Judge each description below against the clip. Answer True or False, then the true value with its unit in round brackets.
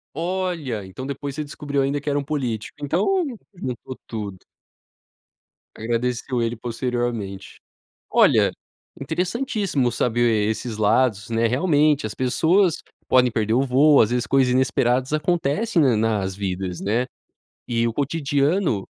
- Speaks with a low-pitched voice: True (130 Hz)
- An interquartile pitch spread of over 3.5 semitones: True (4.6 semitones)